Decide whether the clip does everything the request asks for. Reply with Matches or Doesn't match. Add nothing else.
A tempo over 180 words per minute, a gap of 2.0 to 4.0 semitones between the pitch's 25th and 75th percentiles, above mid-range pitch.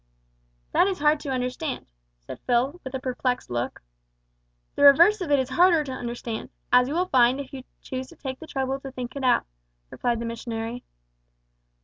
Matches